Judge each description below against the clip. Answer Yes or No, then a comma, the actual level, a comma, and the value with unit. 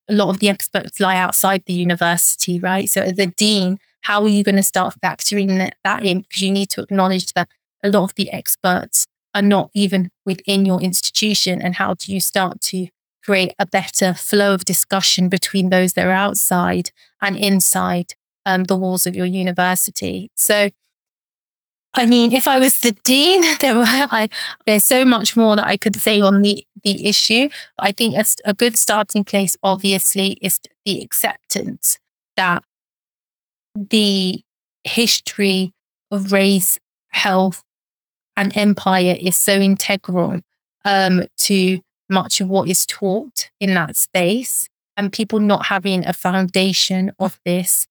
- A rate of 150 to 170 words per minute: Yes, average, 160 wpm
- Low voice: No, high, 195 Hz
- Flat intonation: Yes, narrow, 1.8 semitones